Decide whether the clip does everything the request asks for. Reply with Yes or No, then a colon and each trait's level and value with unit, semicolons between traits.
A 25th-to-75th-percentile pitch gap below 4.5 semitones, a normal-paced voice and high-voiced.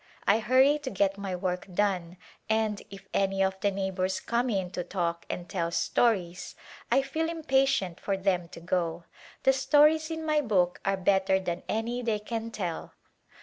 No: average, 5.0 semitones; average, 175 wpm; high, 195 Hz